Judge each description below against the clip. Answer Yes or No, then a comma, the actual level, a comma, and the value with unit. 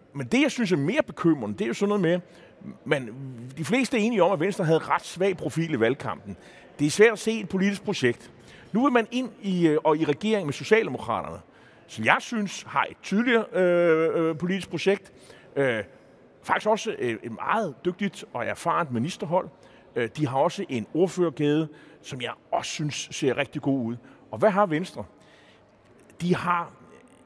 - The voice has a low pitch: No, medium, 175 Hz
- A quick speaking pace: No, average, 180 wpm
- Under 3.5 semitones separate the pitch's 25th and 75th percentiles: No, wide, 5.6 semitones